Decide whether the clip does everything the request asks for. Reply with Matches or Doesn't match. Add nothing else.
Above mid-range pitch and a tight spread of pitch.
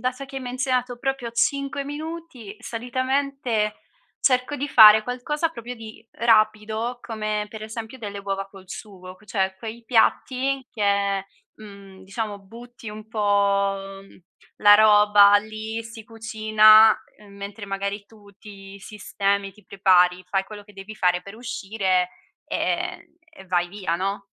Doesn't match